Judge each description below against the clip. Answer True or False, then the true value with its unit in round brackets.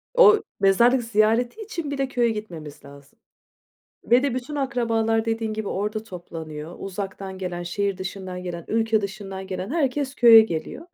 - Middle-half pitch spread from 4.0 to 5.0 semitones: True (4.6 semitones)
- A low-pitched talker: False (215 Hz)